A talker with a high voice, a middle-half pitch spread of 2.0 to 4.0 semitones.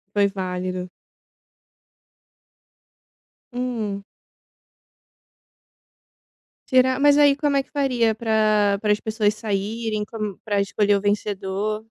Yes: high, 215 Hz; average, 2.8 semitones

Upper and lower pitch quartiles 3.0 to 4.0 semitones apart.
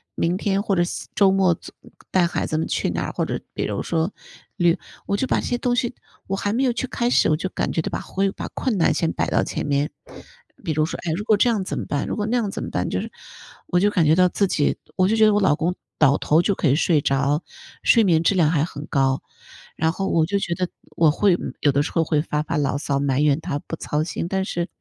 No: average, 4.6 semitones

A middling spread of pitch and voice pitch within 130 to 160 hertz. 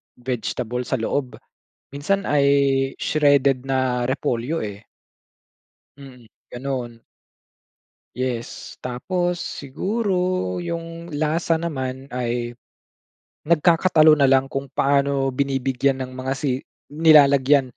Yes: average, 3.1 semitones; low, 135 Hz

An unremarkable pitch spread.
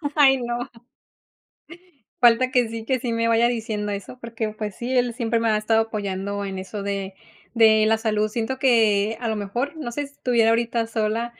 No: narrow, 2.1 semitones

